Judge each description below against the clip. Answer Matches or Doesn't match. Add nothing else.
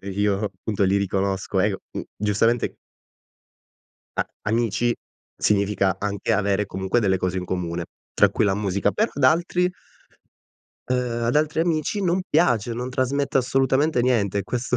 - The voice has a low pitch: Matches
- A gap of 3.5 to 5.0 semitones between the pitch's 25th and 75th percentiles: Matches